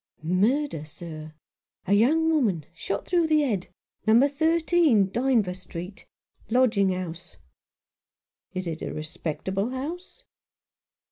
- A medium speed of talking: No, slow, 125 wpm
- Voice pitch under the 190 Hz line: No, high, 210 Hz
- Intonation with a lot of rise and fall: Yes, wide, 8.1 semitones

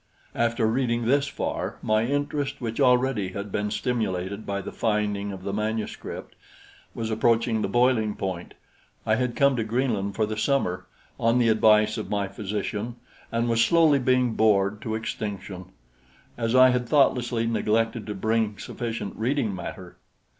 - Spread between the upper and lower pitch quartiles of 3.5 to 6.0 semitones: No, average, 2.8 semitones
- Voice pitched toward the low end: Yes, low, 110 Hz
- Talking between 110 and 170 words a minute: Yes, average, 155 wpm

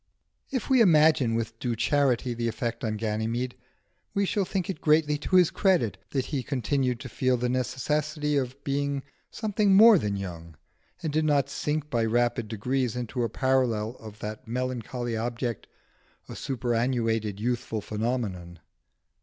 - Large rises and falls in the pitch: No, average, 4.3 semitones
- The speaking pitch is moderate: No, low, 125 Hz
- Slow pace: No, average, 155 wpm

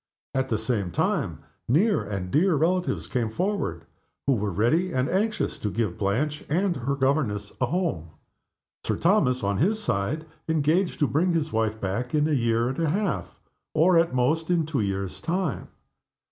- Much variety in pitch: Yes, wide, 7.2 semitones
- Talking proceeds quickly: No, average, 175 wpm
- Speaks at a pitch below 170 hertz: Yes, medium, 140 Hz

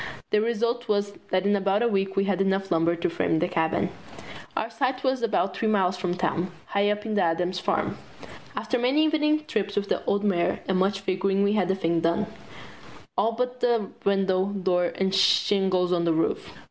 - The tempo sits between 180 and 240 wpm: Yes, average, 200 wpm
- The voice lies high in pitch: Yes, high, 195 Hz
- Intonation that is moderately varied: Yes, average, 3.1 semitones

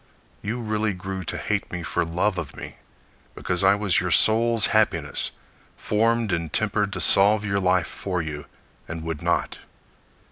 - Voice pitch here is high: No, very low, 95 Hz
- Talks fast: No, average, 165 wpm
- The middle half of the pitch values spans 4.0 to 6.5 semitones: No, average, 3.3 semitones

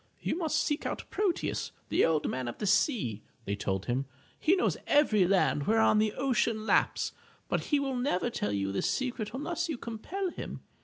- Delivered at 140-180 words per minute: No, average, 190 wpm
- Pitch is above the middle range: Yes, high, 225 Hz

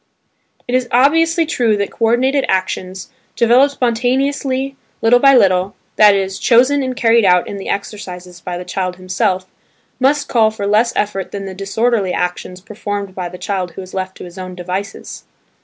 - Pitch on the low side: No, high, 205 Hz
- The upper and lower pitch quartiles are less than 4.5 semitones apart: No, average, 4.9 semitones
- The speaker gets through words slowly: No, average, 175 wpm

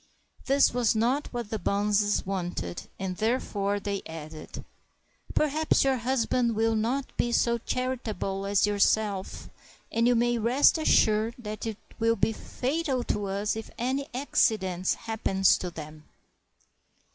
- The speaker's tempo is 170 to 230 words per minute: No, average, 140 wpm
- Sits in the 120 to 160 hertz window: No, high, 220 Hz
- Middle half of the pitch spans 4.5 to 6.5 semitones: No, average, 3.6 semitones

